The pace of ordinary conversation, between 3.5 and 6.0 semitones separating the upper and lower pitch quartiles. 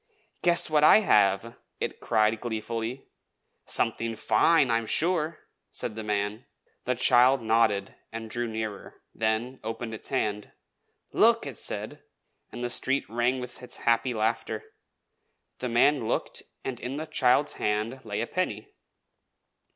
No: average, 145 wpm; average, 3.0 semitones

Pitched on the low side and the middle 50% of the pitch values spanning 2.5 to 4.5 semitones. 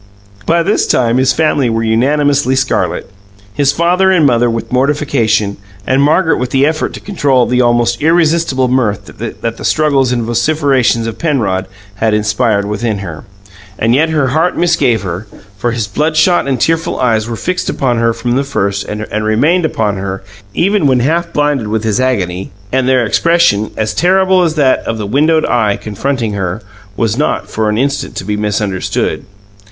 No: low, 125 Hz; wide, 5.5 semitones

